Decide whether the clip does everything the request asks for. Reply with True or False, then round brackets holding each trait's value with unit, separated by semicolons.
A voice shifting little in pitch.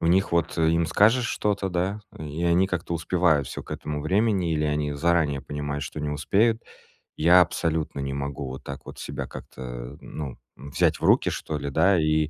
False (3.6 semitones)